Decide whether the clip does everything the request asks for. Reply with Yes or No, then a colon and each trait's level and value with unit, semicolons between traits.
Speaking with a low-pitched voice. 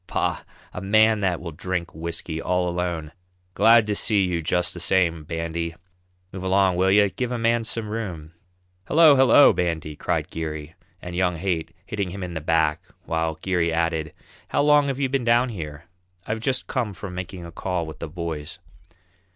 Yes: very low, 90 Hz